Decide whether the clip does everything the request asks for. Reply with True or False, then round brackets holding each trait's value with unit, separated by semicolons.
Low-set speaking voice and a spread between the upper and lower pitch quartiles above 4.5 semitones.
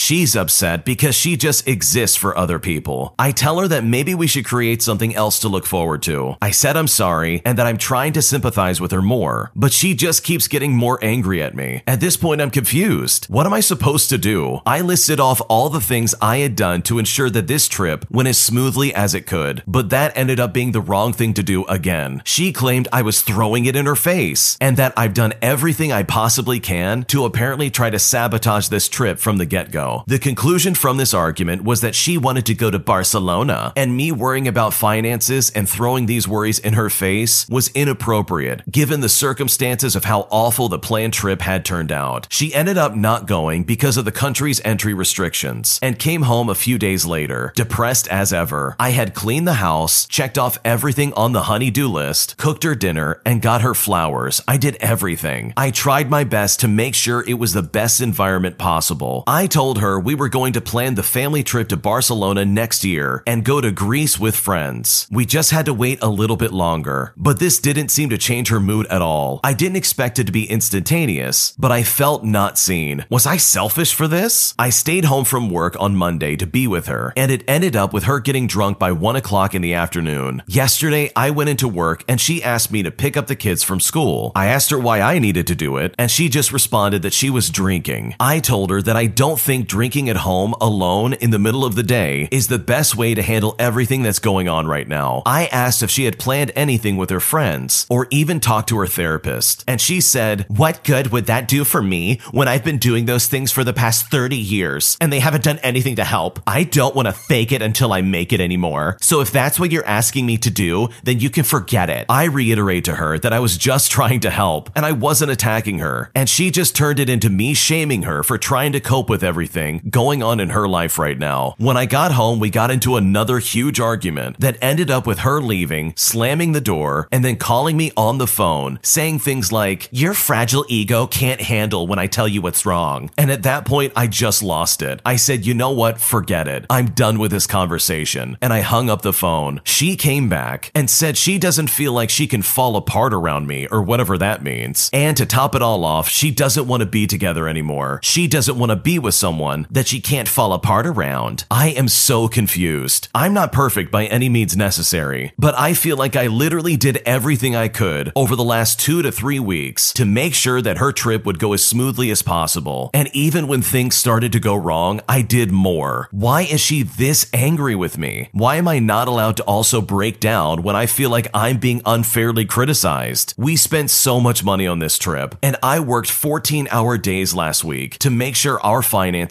True (120 Hz; 5.3 semitones)